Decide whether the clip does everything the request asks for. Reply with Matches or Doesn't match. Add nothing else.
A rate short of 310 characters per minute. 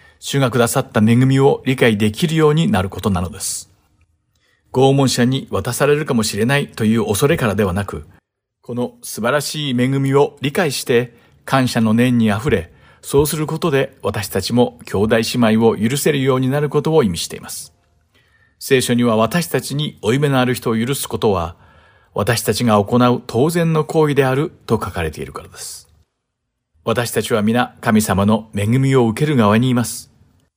Doesn't match